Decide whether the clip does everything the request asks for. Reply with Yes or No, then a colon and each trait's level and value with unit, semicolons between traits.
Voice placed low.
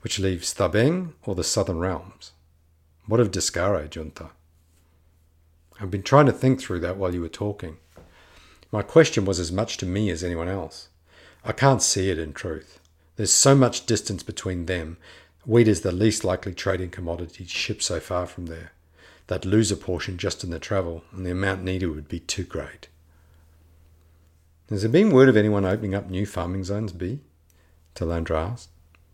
Yes: very low, 90 Hz